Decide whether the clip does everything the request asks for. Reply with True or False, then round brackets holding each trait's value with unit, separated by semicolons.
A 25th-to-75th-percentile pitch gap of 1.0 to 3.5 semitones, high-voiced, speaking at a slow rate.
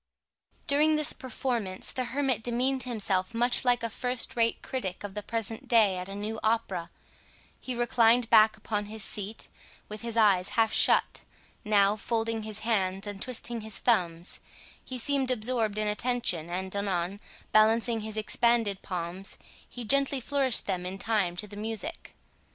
False (3.2 semitones; 220 Hz; 160 wpm)